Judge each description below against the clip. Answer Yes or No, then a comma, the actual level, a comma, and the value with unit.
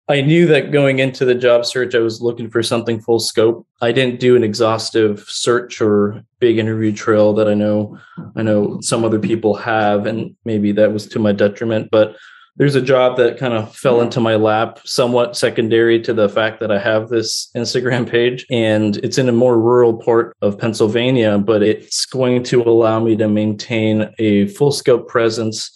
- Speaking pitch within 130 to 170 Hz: No, low, 115 Hz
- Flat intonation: Yes, narrow, 2.0 semitones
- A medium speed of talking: Yes, average, 195 wpm